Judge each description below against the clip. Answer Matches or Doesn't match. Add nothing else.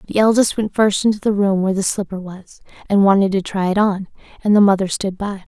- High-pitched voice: Matches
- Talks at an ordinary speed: Doesn't match